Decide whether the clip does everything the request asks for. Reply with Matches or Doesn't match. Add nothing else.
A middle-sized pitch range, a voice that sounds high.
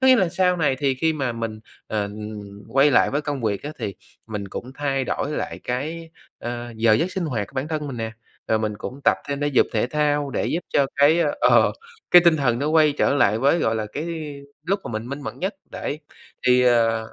Doesn't match